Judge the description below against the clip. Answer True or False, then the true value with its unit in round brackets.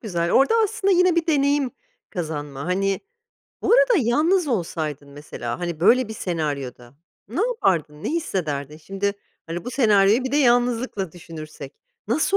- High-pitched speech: True (195 Hz)